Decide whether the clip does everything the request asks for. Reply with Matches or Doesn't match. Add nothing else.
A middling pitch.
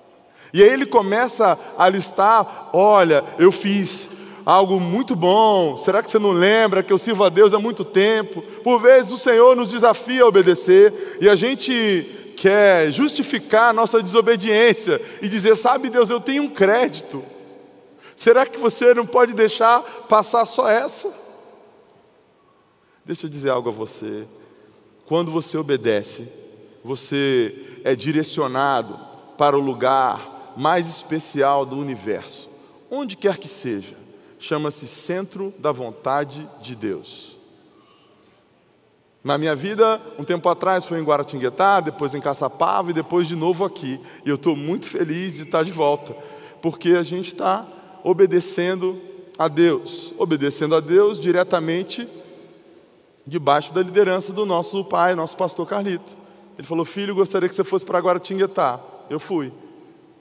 Doesn't match